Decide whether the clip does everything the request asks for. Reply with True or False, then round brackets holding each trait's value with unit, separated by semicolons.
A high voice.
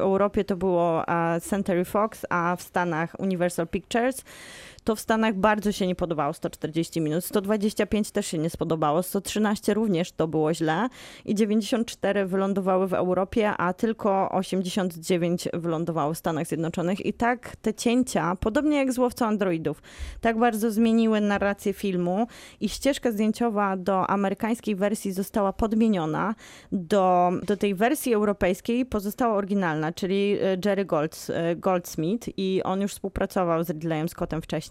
True (195 Hz)